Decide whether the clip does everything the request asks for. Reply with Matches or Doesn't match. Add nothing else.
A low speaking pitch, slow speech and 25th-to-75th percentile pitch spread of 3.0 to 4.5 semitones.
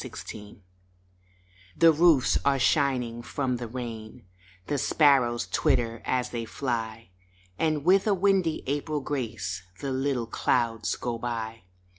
Matches